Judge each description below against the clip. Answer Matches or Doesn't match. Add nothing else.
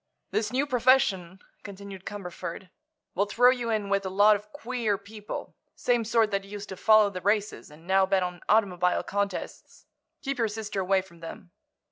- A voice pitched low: Doesn't match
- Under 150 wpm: Doesn't match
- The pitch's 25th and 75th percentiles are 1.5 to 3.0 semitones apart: Matches